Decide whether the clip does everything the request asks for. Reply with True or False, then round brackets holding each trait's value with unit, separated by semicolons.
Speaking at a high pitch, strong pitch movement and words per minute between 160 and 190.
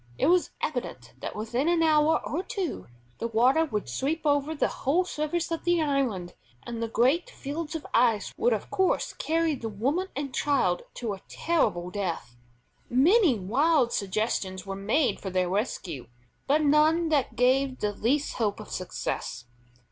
True (265 Hz; 7.2 semitones; 165 wpm)